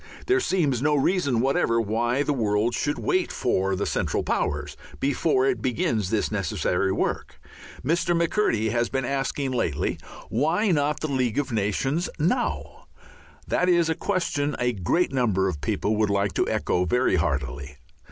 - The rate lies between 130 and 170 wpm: Yes, average, 160 wpm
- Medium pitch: No, low, 125 Hz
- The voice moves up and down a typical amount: No, wide, 6.5 semitones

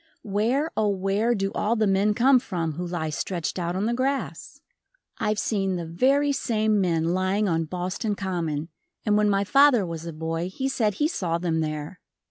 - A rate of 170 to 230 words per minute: Yes, average, 190 wpm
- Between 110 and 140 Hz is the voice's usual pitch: No, high, 195 Hz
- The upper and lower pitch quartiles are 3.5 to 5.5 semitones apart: Yes, average, 4.3 semitones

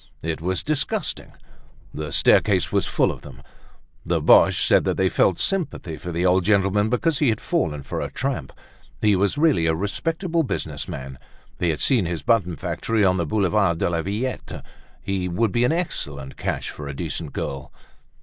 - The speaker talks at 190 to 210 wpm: No, average, 180 wpm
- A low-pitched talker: Yes, very low, 95 Hz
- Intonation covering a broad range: Yes, wide, 6.5 semitones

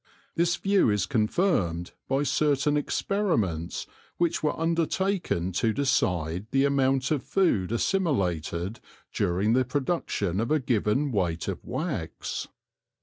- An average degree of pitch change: No, wide, 8.6 semitones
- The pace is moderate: No, slow, 120 wpm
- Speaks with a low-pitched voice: Yes, low, 130 Hz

